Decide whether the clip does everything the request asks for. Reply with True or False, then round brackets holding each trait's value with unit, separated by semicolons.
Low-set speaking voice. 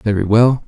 True (110 Hz)